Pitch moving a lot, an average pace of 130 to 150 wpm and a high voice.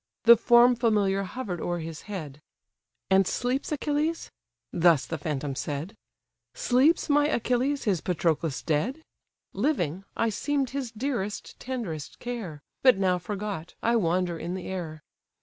Yes: wide, 6.9 semitones; slow, 135 wpm; high, 200 Hz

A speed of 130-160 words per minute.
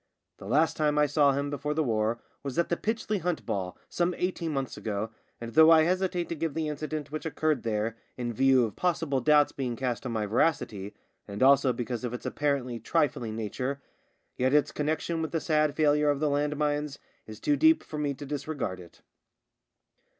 No: average, 200 wpm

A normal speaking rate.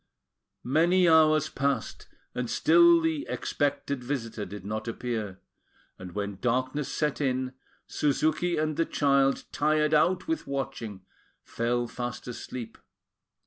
No: slow, 120 wpm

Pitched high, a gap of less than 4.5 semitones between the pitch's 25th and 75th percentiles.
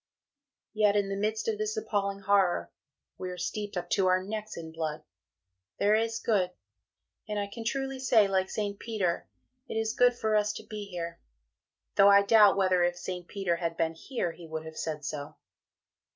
Yes: high, 200 Hz; average, 3.4 semitones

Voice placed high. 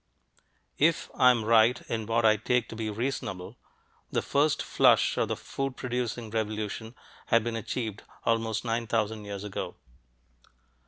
No: low, 115 Hz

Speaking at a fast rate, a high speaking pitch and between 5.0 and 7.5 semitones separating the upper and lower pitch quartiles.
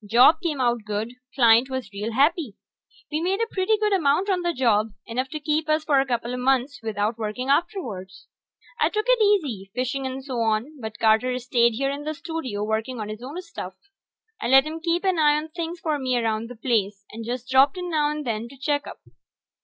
Yes: fast, 215 wpm; very high, 260 Hz; wide, 5.4 semitones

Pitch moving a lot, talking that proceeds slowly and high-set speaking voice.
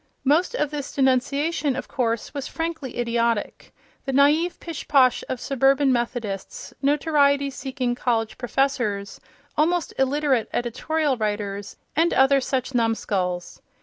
No: average, 3.5 semitones; slow, 115 wpm; very high, 265 Hz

